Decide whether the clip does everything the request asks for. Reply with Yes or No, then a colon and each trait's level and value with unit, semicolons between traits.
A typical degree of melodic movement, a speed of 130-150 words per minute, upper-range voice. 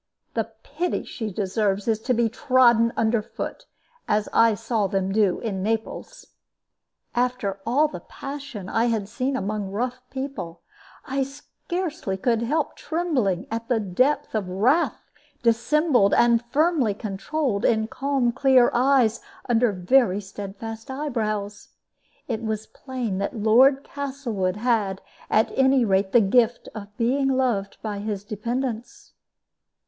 Yes: average, 4.2 semitones; slow, 135 wpm; high, 230 Hz